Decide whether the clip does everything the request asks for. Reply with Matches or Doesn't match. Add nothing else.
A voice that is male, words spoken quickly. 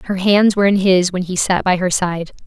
Doesn't match